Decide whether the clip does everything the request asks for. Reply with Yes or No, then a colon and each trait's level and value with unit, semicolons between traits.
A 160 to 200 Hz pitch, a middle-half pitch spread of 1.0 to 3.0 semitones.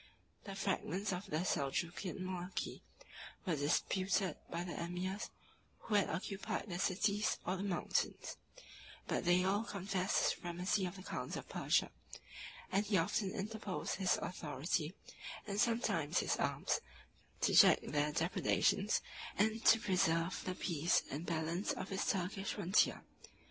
Yes: medium, 185 Hz; narrow, 2.5 semitones